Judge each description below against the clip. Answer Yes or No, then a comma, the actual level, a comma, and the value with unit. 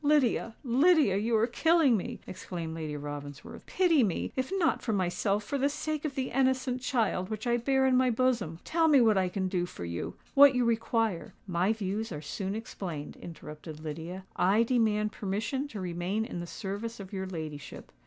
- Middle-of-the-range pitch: No, high, 215 Hz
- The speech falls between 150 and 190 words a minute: Yes, average, 180 wpm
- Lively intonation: Yes, wide, 6.3 semitones